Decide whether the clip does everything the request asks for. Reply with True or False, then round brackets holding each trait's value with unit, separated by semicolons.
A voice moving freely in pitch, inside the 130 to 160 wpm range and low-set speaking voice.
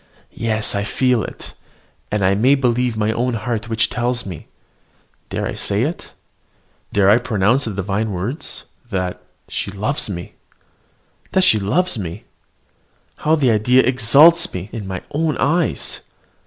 False (4.4 semitones; 150 wpm; 115 Hz)